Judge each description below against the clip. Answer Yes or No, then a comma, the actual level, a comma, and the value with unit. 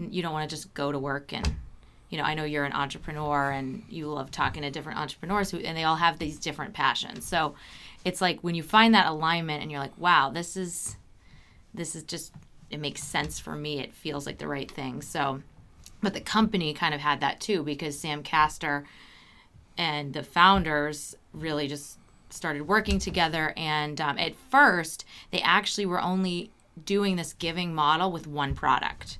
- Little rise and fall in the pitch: No, average, 3.2 semitones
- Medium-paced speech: Yes, average, 195 wpm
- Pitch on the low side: No, medium, 155 Hz